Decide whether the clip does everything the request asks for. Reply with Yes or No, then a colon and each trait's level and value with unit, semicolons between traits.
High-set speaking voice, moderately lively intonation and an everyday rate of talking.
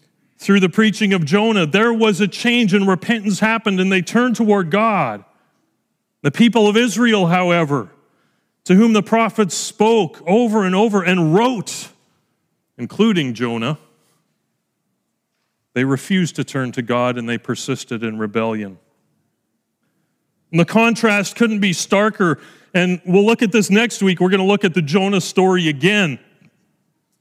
Yes: high, 195 Hz; average, 4.6 semitones; average, 150 wpm